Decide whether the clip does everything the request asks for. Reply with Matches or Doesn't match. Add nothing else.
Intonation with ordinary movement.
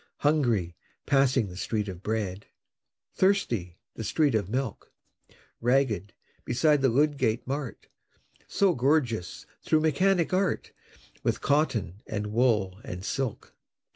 Doesn't match